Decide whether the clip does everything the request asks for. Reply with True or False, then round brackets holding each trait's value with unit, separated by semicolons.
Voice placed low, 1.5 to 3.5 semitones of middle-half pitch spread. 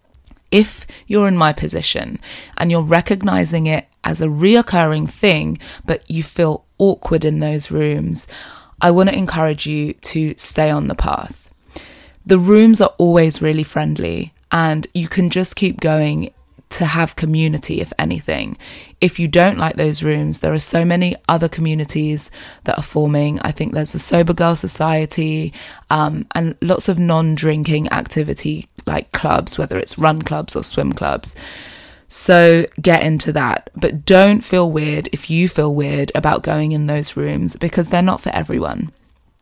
False (155 Hz; 2.4 semitones)